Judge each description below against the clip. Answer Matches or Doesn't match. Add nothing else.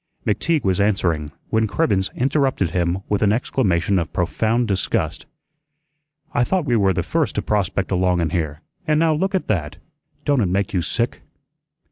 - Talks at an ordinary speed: Matches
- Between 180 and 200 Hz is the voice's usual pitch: Doesn't match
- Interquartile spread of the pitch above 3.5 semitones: Matches